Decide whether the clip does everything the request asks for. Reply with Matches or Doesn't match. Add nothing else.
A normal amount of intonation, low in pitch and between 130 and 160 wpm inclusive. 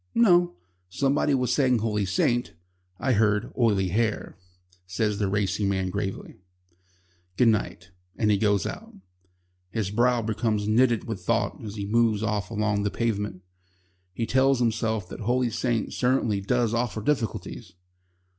Matches